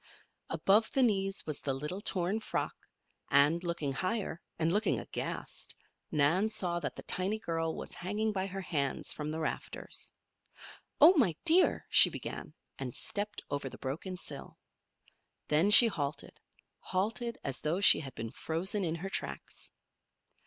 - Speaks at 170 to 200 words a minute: No, average, 150 wpm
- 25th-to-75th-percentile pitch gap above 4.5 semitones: Yes, average, 5.2 semitones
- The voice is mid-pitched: Yes, medium, 180 Hz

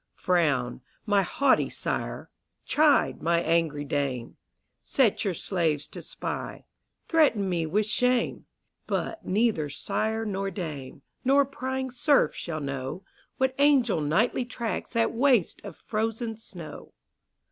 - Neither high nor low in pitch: No, high, 205 Hz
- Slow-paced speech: Yes, slow, 125 wpm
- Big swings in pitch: Yes, wide, 7.6 semitones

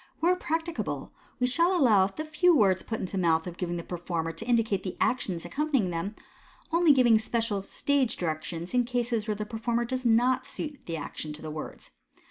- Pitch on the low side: No, high, 225 Hz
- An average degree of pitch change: No, wide, 6.4 semitones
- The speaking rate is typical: Yes, average, 190 wpm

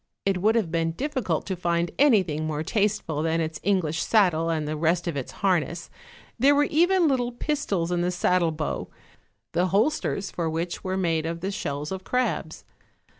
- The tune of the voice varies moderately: Yes, average, 4.5 semitones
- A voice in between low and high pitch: Yes, medium, 175 Hz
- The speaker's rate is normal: Yes, average, 180 wpm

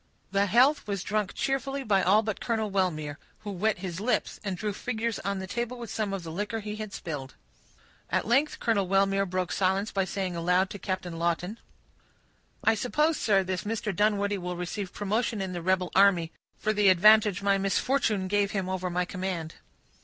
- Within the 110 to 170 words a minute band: No, average, 190 wpm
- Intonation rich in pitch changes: No, average, 2.7 semitones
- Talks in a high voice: Yes, high, 195 Hz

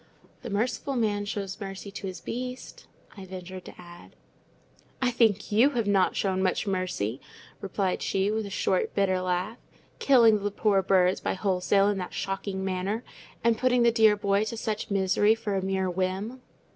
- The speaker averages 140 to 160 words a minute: No, average, 175 wpm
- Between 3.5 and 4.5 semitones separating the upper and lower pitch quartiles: No, narrow, 2.6 semitones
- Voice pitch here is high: Yes, high, 200 Hz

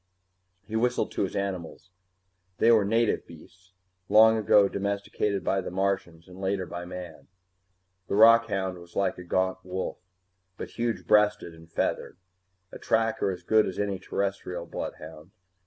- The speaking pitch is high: No, very low, 95 Hz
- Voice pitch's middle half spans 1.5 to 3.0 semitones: Yes, average, 2.7 semitones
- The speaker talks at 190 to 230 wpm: No, average, 150 wpm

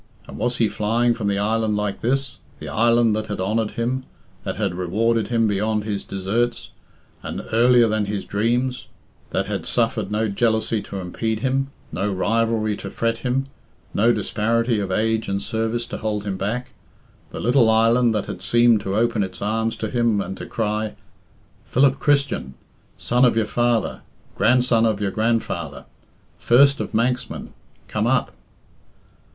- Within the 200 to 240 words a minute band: No, average, 165 wpm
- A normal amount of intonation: No, narrow, 2.3 semitones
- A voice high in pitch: No, low, 110 Hz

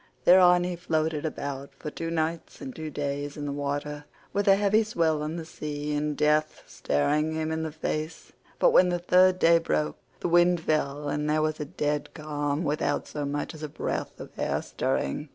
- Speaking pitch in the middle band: Yes, medium, 155 Hz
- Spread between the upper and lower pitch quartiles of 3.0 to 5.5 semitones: No, narrow, 2.4 semitones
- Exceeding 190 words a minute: Yes, average, 200 wpm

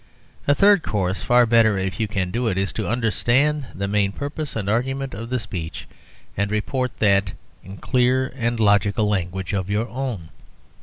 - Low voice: Yes, low, 110 Hz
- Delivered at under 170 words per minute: No, average, 175 wpm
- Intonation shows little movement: No, average, 4.3 semitones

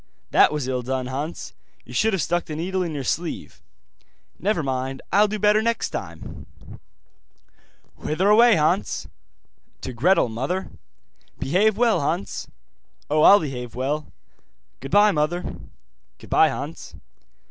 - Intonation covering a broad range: Yes, wide, 7.0 semitones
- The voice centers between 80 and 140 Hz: No, medium, 165 Hz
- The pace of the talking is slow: Yes, slow, 130 wpm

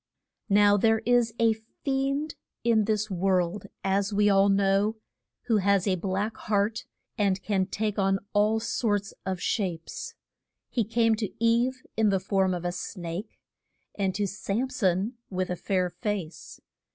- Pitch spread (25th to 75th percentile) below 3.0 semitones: Yes, narrow, 2.6 semitones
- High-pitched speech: Yes, high, 205 Hz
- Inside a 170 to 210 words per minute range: No, average, 150 wpm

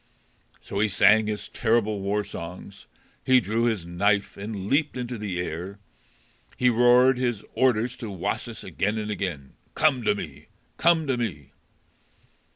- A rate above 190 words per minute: No, average, 150 wpm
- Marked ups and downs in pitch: No, average, 3.7 semitones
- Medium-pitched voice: No, low, 105 Hz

